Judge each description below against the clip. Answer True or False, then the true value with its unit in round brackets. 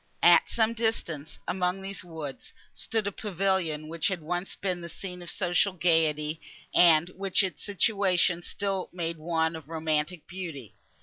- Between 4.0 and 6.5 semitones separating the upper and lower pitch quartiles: False (3.0 semitones)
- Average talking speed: True (150 wpm)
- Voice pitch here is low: False (175 Hz)